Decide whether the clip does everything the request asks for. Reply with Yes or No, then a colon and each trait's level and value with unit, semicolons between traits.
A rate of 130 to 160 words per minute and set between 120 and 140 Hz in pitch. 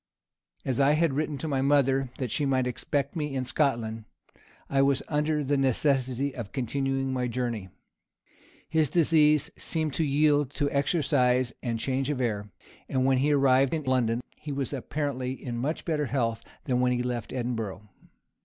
No: average, 170 wpm; low, 135 Hz